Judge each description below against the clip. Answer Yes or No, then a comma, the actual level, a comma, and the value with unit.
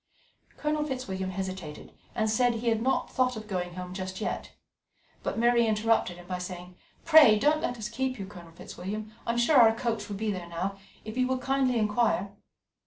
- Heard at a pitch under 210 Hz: No, high, 215 Hz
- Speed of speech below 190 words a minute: No, average, 195 wpm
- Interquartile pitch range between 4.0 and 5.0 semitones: Yes, average, 4.5 semitones